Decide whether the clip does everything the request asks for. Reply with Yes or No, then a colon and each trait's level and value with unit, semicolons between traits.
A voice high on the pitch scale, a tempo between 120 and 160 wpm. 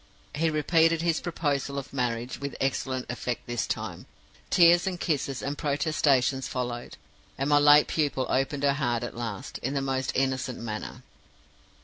No: low, 135 Hz; average, 155 wpm